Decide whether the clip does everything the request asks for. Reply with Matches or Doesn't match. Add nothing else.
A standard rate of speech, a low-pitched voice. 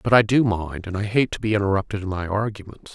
Doesn't match